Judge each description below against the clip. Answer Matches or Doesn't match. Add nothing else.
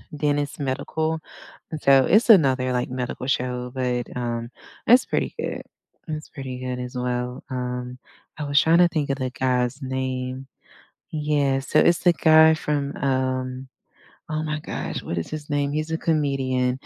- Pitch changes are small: Doesn't match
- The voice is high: Doesn't match